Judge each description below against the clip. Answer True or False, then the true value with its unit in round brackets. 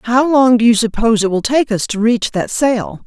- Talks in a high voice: True (230 Hz)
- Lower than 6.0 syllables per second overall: True (5.0 syllables/s)